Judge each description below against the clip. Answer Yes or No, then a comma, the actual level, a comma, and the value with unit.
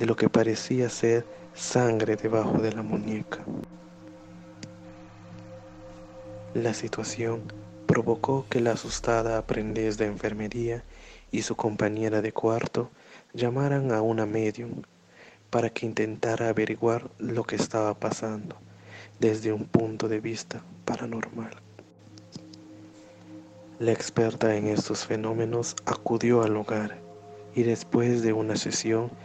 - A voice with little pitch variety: Yes, narrow, 1.5 semitones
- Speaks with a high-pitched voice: No, low, 110 Hz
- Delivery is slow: Yes, slow, 115 wpm